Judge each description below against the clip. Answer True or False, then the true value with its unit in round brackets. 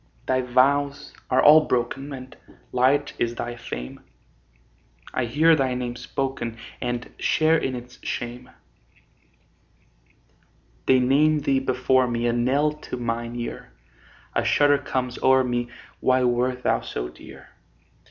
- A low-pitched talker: True (125 Hz)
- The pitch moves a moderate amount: False (2.2 semitones)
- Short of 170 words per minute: True (135 wpm)